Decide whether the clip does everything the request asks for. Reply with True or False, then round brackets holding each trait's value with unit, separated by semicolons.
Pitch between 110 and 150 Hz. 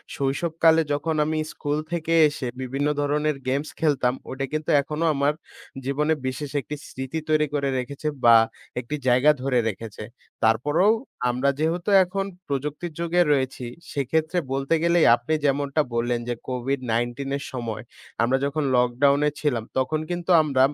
True (140 Hz)